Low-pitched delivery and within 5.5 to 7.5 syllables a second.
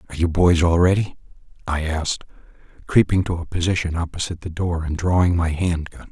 Yes: very low, 85 Hz; 6.0 syllables/s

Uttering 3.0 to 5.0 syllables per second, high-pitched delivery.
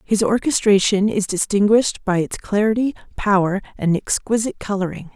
No: 5.4 syllables/s; high, 205 Hz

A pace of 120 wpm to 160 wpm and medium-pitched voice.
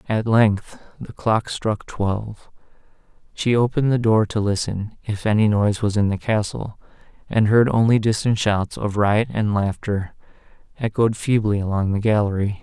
No: average, 155 wpm; low, 105 Hz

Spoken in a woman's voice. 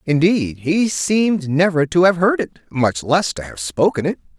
No: male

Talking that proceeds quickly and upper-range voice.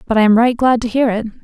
Yes: fast, 335 wpm; high, 230 Hz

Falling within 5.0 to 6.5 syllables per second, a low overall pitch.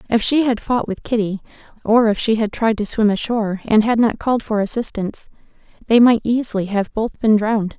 No: 5.7 syllables/s; high, 220 Hz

